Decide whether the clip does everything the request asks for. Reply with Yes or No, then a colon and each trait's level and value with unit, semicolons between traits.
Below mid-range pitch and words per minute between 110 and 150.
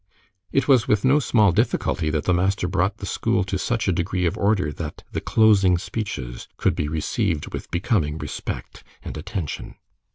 No: very low, 95 Hz; average, 175 wpm